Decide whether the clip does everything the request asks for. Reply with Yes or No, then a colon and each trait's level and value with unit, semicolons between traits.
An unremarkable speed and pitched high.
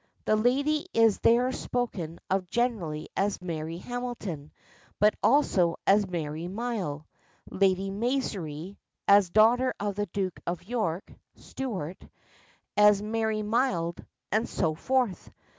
No: slow, 120 wpm; high, 205 Hz